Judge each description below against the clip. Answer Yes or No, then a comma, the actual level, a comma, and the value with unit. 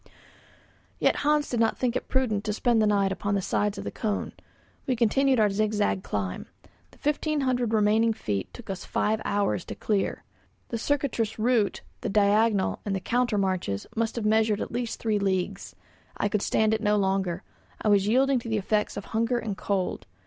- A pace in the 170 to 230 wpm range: Yes, average, 190 wpm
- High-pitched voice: Yes, high, 215 Hz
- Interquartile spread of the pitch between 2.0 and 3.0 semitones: Yes, average, 2.7 semitones